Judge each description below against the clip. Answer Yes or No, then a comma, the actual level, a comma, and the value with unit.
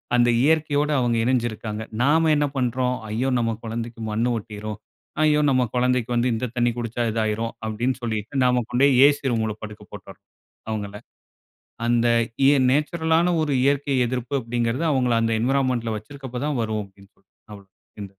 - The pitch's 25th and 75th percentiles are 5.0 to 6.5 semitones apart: No, average, 3.2 semitones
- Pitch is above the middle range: No, low, 120 Hz